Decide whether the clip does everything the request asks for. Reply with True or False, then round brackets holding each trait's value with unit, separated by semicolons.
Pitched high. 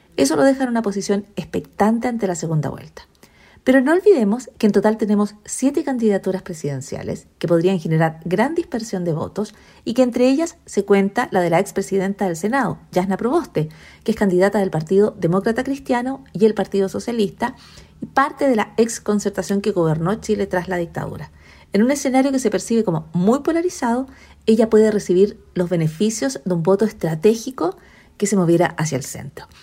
True (205 Hz)